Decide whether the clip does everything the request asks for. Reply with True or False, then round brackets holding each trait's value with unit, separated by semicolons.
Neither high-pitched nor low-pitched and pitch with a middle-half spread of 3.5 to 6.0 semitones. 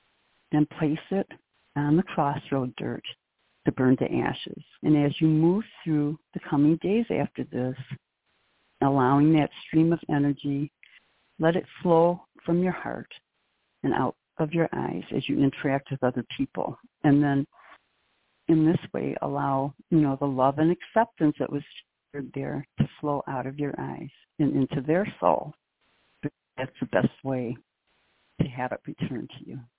False (145 Hz; 3.1 semitones)